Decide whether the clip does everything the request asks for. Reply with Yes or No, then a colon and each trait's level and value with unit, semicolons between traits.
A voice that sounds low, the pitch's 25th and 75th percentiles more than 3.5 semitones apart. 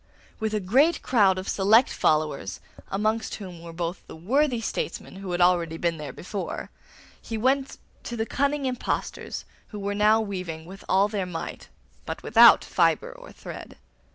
No: high, 200 Hz; average, 4.4 semitones